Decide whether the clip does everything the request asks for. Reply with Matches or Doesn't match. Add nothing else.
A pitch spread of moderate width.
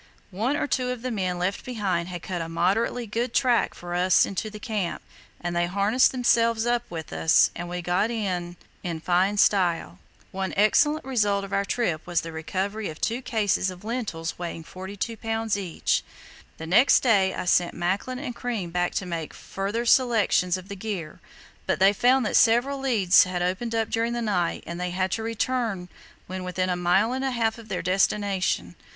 Matches